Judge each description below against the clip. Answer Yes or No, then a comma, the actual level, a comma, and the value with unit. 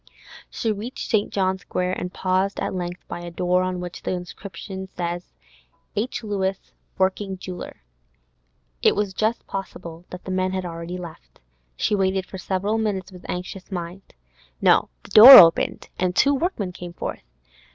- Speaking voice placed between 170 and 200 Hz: Yes, medium, 185 Hz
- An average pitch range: No, narrow, 1.9 semitones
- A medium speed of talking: Yes, average, 160 wpm